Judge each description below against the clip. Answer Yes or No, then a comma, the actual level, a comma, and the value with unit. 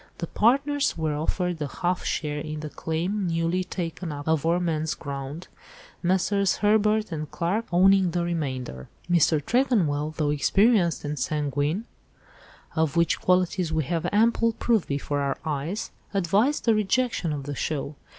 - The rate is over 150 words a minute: No, average, 145 wpm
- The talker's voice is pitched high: No, medium, 170 Hz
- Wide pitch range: No, average, 4.6 semitones